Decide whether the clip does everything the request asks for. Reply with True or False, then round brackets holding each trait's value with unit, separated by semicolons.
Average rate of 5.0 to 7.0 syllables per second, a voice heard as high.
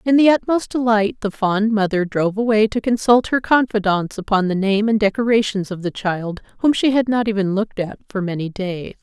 True (5.4 syllables/s; 210 Hz)